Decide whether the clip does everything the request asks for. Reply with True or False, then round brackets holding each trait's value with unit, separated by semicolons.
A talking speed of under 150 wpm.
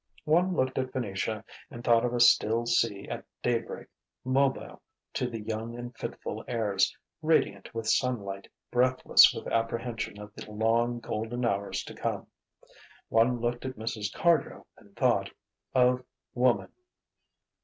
True (140 wpm)